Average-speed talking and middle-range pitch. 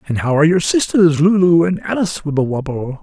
Yes: average, 180 wpm; medium, 165 Hz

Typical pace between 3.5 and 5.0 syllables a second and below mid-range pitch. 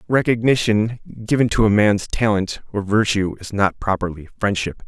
Yes: 4.7 syllables/s; low, 105 Hz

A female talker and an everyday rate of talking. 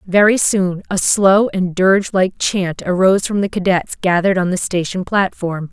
Yes: female; average, 180 wpm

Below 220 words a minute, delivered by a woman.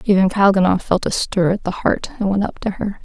No: fast, 255 wpm; female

